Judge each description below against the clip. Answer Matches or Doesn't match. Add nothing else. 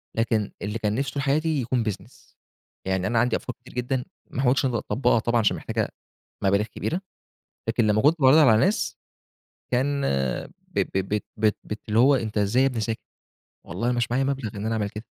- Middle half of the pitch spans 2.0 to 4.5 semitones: Matches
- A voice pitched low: Matches